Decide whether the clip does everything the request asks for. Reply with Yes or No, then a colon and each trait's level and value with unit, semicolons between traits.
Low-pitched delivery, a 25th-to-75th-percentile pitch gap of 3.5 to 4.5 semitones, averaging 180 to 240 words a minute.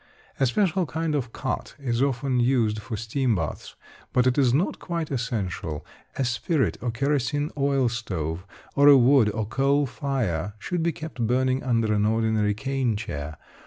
No: low, 125 Hz; average, 4.2 semitones; average, 165 wpm